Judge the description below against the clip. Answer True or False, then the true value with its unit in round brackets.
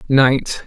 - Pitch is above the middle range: False (135 Hz)